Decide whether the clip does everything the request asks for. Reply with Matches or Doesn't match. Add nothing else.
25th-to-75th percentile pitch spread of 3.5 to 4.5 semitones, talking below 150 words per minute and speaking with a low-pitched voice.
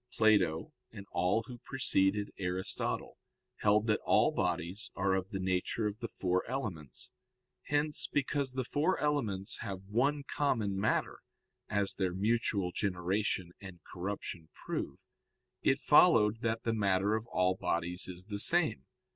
Matches